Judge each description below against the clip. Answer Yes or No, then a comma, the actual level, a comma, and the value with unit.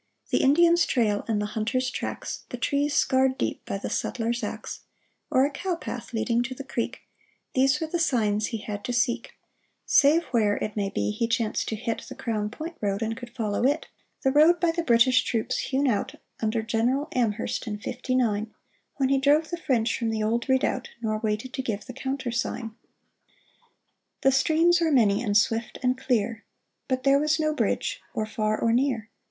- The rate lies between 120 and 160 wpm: No, average, 195 wpm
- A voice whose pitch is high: Yes, high, 245 Hz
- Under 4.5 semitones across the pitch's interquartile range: Yes, average, 3.7 semitones